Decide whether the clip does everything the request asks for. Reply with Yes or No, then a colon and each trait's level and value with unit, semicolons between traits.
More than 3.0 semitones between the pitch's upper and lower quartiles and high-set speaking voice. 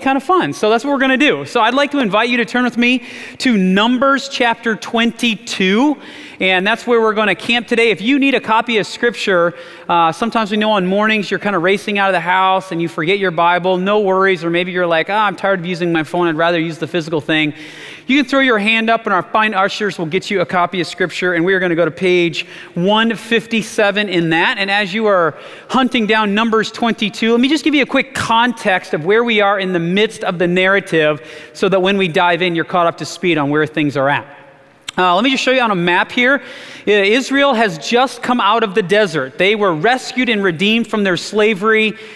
Yes: average, 4.7 semitones; high, 205 Hz